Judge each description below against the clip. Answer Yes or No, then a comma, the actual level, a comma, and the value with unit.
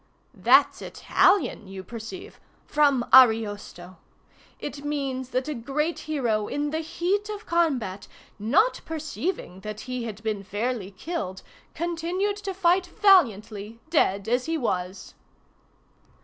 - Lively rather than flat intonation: Yes, wide, 8.1 semitones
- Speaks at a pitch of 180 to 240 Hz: No, very high, 260 Hz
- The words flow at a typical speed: No, slow, 120 wpm